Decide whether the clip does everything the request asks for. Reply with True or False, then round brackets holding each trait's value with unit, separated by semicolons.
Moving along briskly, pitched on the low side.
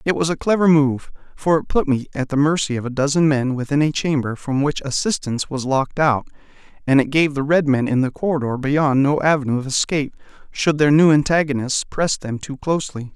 False (215 wpm; 145 Hz)